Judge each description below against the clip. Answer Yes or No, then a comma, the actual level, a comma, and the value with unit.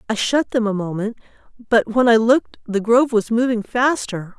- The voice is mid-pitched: No, high, 230 Hz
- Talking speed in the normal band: Yes, average, 190 wpm